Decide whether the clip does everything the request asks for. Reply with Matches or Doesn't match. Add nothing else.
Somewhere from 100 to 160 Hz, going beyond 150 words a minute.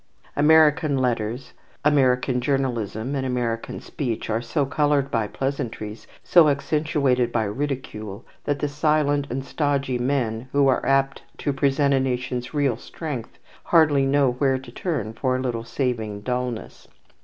Doesn't match